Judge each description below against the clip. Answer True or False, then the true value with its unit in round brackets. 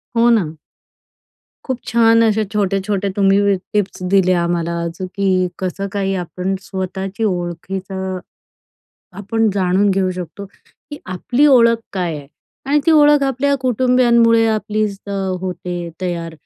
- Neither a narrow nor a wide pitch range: True (3.7 semitones)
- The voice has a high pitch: True (195 Hz)